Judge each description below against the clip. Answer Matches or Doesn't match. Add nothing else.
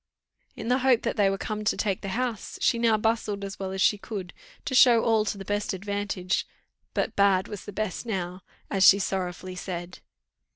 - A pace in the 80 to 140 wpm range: Doesn't match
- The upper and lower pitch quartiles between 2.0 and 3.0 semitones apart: Matches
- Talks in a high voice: Matches